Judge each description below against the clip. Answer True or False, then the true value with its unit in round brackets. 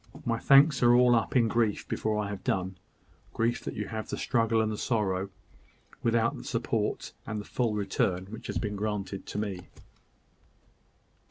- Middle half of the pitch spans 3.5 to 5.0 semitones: False (2.4 semitones)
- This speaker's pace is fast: False (175 wpm)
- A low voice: True (110 Hz)